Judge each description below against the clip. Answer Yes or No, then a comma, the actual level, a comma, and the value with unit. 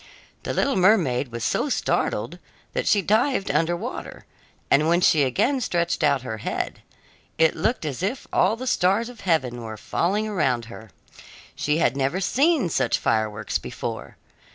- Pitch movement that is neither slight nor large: No, wide, 8.7 semitones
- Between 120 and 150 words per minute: No, average, 160 wpm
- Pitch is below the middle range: No, medium, 170 Hz